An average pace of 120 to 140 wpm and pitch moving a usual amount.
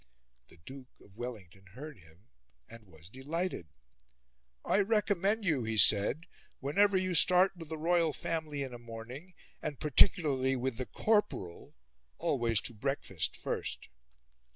No: slow, 135 wpm; wide, 7.3 semitones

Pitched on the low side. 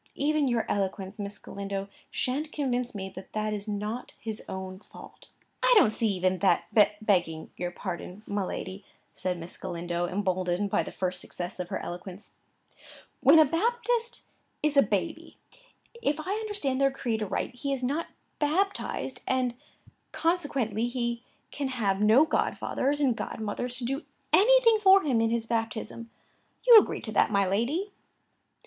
No: high, 230 Hz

